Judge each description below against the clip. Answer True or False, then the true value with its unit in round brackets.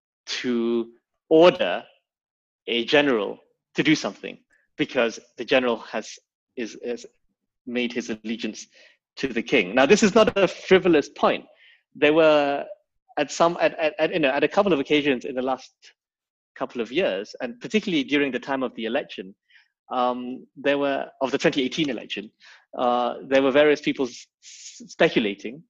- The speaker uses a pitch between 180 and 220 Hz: False (140 Hz)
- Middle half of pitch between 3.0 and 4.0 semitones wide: False (4.5 semitones)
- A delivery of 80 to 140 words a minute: False (160 wpm)